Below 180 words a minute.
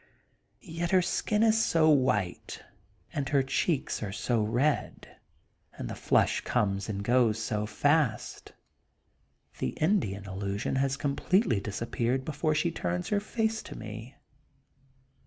Yes: slow, 135 wpm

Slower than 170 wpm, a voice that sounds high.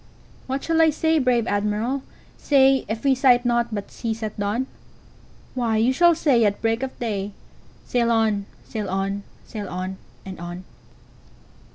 Yes: average, 145 wpm; high, 230 Hz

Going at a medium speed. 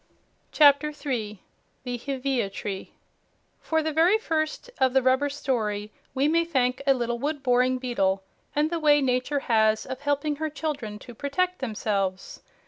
Yes: average, 155 wpm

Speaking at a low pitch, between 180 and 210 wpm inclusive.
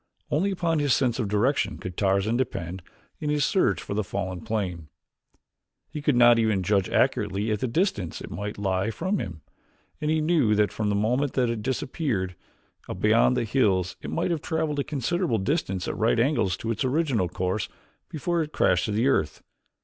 Yes: low, 115 Hz; average, 190 wpm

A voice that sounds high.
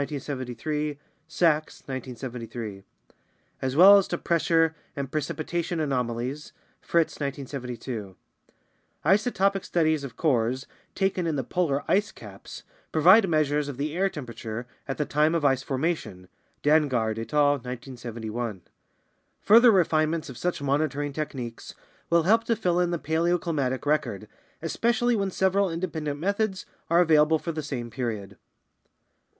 No: medium, 150 Hz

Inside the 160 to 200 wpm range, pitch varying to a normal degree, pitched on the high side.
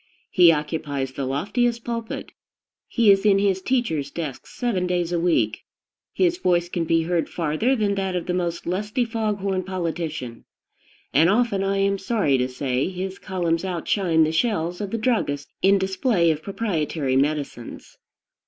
No: average, 165 wpm; average, 4.1 semitones; medium, 180 Hz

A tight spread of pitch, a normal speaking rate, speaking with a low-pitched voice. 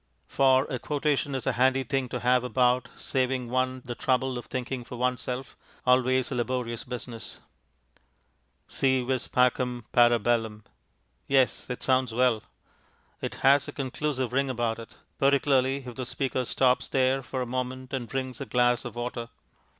Yes: narrow, 1.4 semitones; average, 160 wpm; low, 125 Hz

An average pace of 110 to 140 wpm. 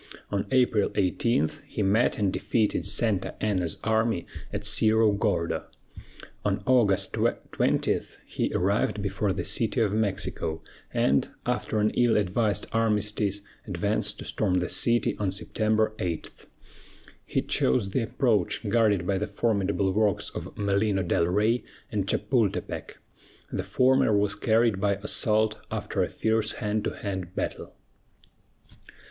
Yes: slow, 135 wpm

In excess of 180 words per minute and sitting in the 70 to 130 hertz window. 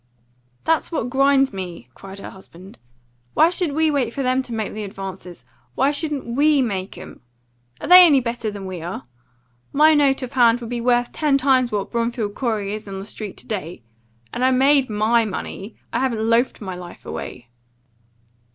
No: average, 190 wpm; high, 235 Hz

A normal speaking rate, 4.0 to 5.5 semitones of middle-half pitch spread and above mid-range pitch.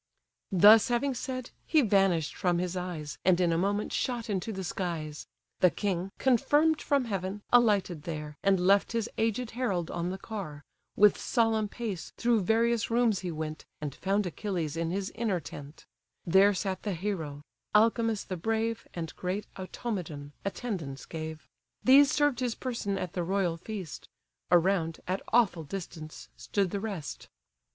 Yes: average, 160 wpm; average, 4.7 semitones; high, 195 Hz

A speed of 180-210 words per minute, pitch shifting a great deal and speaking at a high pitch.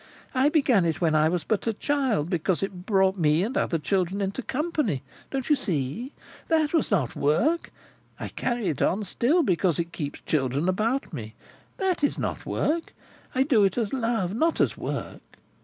Yes: average, 185 wpm; wide, 8.0 semitones; high, 200 Hz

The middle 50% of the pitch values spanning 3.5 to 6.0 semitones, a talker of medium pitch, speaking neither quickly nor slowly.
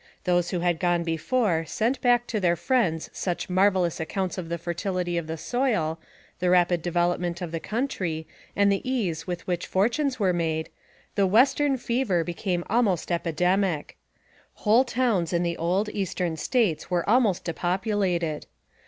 Yes: average, 3.9 semitones; medium, 180 Hz; average, 170 wpm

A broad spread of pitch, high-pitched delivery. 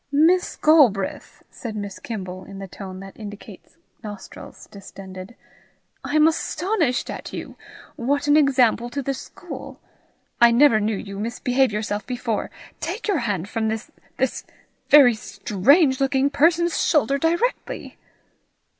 Yes: wide, 5.9 semitones; high, 240 Hz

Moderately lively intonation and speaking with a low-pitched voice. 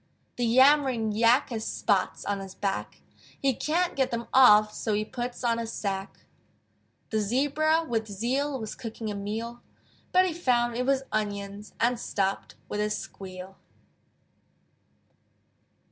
No: average, 3.9 semitones; high, 230 Hz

